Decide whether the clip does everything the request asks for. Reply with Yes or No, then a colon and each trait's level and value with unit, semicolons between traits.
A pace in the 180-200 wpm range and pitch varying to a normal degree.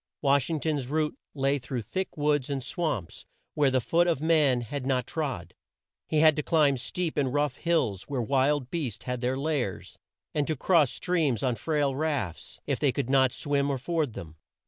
Yes: average, 190 wpm; average, 3.4 semitones